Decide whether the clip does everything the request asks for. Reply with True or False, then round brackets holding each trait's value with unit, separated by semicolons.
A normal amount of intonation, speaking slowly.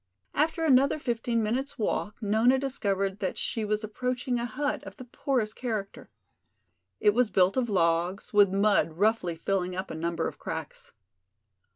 False (4.5 semitones; 160 wpm)